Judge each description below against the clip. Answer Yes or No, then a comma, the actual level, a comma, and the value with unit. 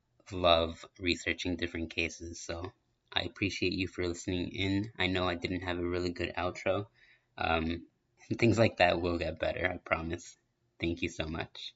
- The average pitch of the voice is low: Yes, very low, 85 Hz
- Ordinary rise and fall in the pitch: No, narrow, 1.3 semitones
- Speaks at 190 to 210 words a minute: No, average, 170 wpm